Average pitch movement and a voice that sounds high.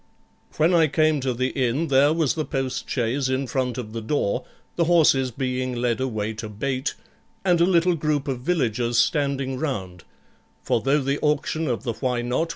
No: average, 3.8 semitones; low, 130 Hz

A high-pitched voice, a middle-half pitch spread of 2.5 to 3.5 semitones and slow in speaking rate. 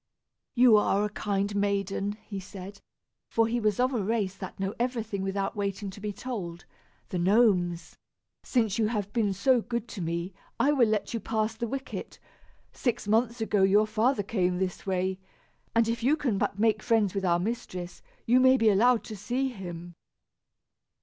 No: high, 210 Hz; average, 3.2 semitones; average, 180 wpm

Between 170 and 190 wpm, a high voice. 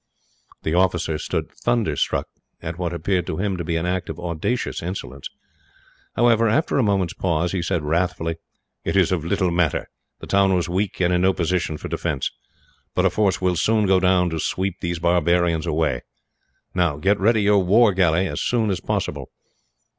No: average, 185 wpm; very low, 90 Hz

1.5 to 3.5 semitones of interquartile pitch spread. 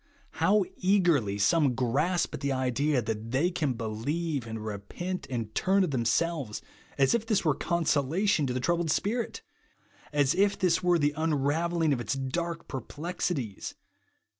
No: average, 5.3 semitones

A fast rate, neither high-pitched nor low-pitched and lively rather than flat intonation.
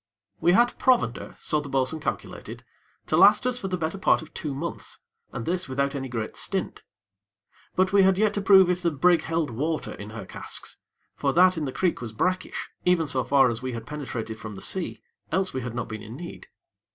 Yes: fast, 215 wpm; medium, 155 Hz; wide, 6.2 semitones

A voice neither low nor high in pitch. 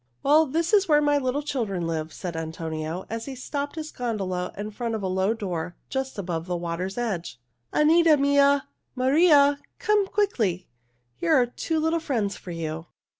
No: high, 235 Hz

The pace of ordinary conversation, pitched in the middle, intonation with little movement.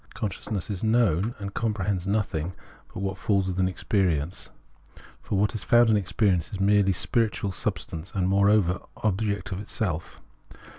No: average, 160 wpm; low, 100 Hz; narrow, 2.3 semitones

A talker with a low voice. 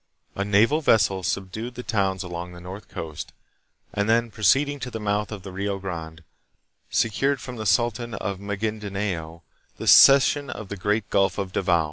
Yes: low, 100 Hz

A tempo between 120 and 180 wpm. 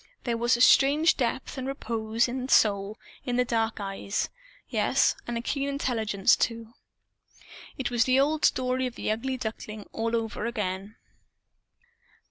Yes: average, 150 wpm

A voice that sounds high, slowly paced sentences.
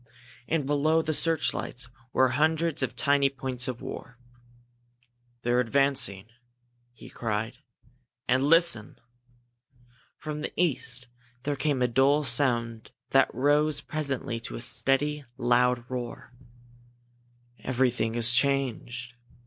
No: low, 130 Hz; slow, 110 wpm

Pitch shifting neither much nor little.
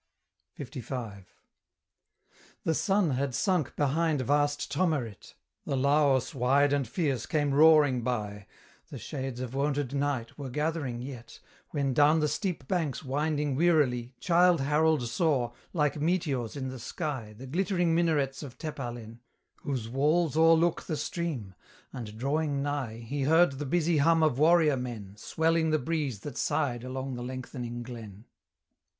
Yes: average, 4.0 semitones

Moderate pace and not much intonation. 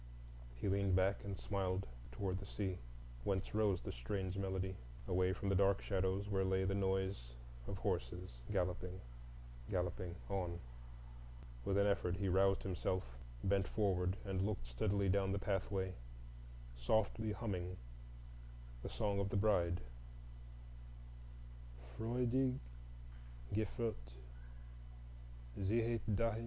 No: slow, 120 wpm; narrow, 1.5 semitones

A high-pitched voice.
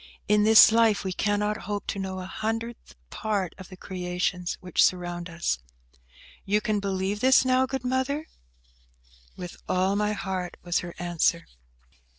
Yes: high, 195 Hz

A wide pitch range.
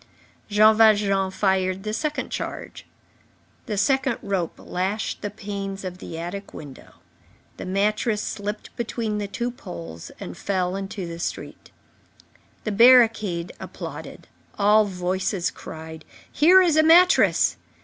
No: average, 2.8 semitones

